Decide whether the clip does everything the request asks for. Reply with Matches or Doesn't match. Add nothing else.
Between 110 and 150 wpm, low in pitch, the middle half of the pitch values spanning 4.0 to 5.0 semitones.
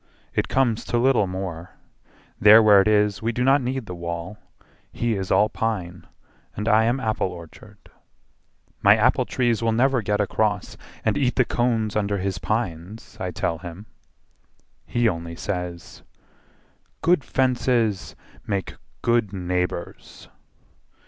Matches